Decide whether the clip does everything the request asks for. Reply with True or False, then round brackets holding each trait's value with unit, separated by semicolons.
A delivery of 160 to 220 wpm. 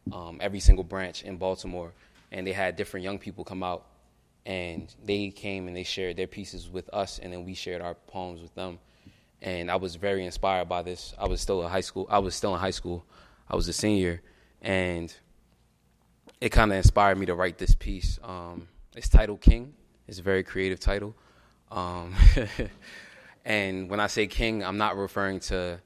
True (195 wpm)